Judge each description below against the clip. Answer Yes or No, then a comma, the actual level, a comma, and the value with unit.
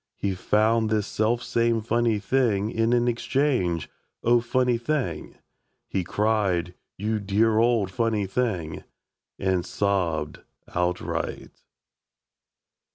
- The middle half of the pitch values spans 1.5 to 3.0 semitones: No, average, 3.7 semitones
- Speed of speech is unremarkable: No, slow, 100 wpm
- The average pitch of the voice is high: No, low, 110 Hz